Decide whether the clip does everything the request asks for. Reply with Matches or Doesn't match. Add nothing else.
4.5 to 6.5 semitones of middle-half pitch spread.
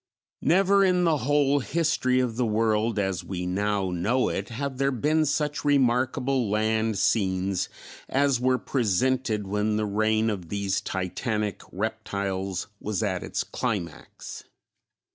Matches